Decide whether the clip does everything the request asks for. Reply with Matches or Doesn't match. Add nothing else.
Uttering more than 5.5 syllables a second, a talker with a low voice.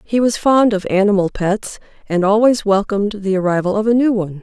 Doesn't match